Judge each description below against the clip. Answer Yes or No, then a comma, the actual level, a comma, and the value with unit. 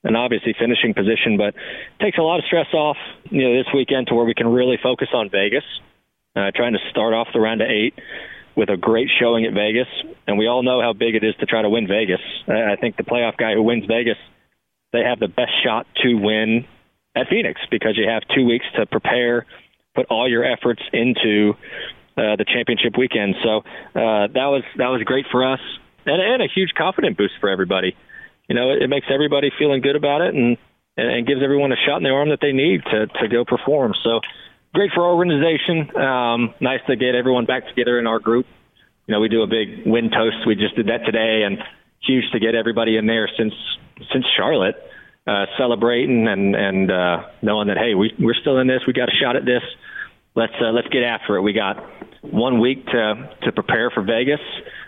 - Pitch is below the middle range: Yes, low, 120 Hz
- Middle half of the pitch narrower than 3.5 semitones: Yes, average, 3.0 semitones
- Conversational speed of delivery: No, fast, 220 wpm